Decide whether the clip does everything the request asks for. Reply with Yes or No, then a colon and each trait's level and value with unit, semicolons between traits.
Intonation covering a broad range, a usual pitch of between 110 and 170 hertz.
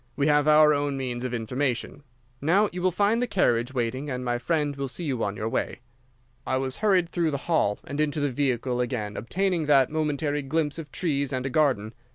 No: average, 3.8 semitones; medium, 140 Hz